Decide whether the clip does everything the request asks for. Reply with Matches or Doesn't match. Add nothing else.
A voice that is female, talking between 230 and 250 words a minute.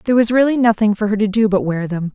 Doesn't match